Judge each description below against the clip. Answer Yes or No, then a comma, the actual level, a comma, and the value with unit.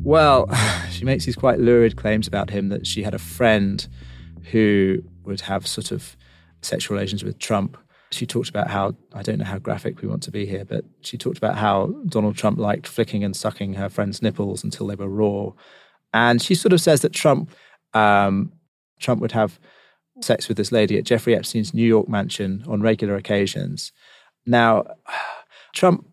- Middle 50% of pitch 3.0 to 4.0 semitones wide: No, narrow, 2.6 semitones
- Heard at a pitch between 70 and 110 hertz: Yes, low, 105 Hz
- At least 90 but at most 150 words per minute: No, average, 180 wpm